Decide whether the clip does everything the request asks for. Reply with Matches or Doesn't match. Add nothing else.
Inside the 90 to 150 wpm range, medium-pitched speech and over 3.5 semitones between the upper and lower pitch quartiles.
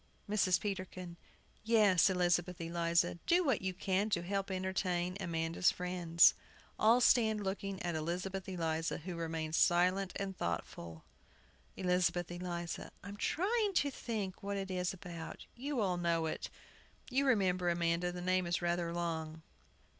Doesn't match